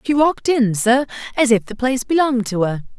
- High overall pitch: Yes, high, 245 Hz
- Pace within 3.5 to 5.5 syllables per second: No, 6.2 syllables/s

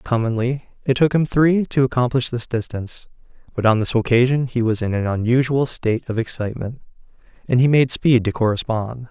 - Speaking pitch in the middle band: No, low, 120 Hz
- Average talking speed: Yes, average, 180 wpm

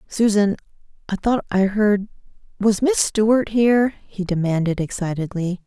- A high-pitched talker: Yes, high, 205 Hz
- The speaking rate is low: Yes, slow, 115 wpm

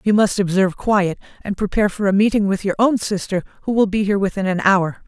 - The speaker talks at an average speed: No, fast, 235 wpm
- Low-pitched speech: No, high, 200 Hz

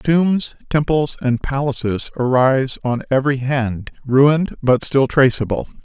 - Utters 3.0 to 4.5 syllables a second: Yes, 4.3 syllables/s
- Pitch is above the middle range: No, low, 135 Hz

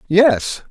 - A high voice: No, medium, 170 Hz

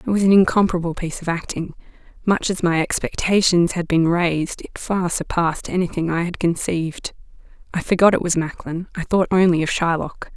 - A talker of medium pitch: Yes, medium, 175 Hz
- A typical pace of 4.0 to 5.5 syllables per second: No, 5.7 syllables/s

